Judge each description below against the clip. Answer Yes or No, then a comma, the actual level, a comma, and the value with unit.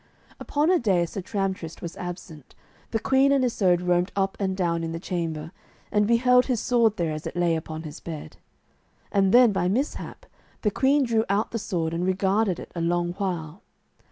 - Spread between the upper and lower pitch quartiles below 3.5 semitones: No, average, 4.7 semitones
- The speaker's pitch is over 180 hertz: Yes, high, 190 Hz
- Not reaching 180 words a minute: No, average, 195 wpm